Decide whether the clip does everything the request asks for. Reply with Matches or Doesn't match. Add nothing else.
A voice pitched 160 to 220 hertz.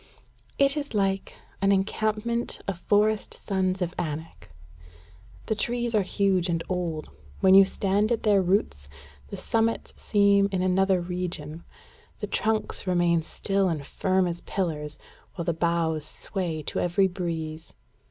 Matches